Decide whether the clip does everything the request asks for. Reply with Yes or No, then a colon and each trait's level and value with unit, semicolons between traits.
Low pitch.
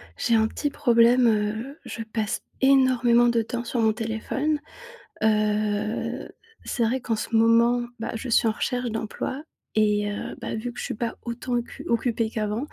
No: high, 230 Hz